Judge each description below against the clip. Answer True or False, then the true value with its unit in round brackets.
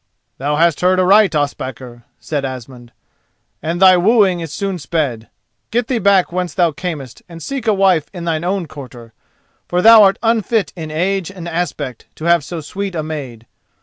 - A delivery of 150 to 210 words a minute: True (180 wpm)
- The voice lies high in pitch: False (170 Hz)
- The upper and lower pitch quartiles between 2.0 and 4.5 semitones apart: False (4.9 semitones)